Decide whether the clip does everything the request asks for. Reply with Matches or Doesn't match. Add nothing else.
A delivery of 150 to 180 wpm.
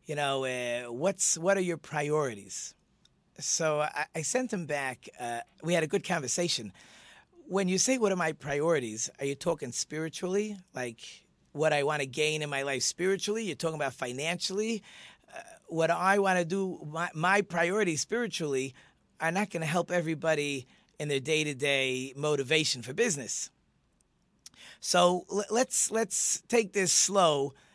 Matches